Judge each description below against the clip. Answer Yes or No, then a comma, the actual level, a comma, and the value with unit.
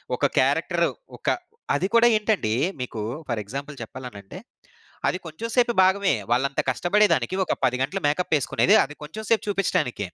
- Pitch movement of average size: No, wide, 8.0 semitones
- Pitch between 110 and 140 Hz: No, medium, 155 Hz